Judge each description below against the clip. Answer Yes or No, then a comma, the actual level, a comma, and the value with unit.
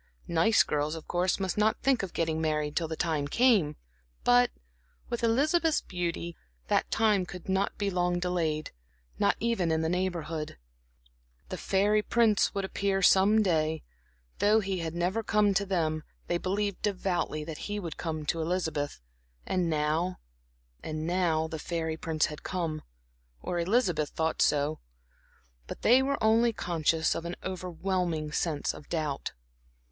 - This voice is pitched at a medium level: Yes, medium, 175 Hz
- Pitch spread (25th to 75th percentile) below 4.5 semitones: Yes, average, 4.0 semitones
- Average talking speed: Yes, average, 155 wpm